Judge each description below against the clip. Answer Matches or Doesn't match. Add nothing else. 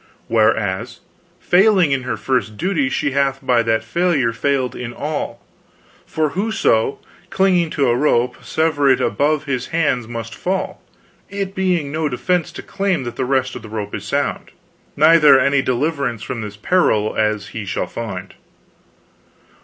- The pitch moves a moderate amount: Doesn't match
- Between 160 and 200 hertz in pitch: Doesn't match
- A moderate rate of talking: Matches